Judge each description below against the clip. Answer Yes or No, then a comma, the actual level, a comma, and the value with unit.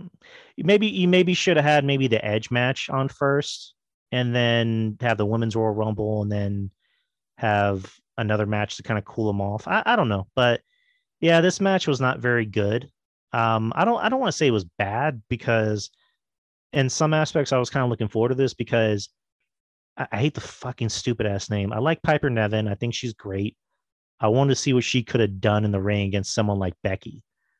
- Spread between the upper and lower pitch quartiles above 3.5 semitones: Yes, average, 4.6 semitones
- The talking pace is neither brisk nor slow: No, fast, 215 wpm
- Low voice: Yes, low, 115 Hz